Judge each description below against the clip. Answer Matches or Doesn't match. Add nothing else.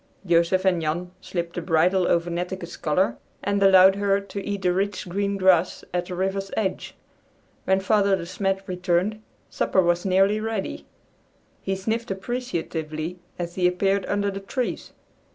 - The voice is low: Doesn't match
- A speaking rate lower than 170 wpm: Matches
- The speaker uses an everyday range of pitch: Doesn't match